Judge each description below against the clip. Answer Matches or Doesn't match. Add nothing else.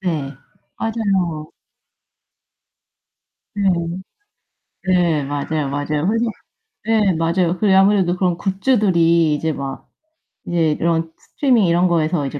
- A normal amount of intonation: Matches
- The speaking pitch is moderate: Matches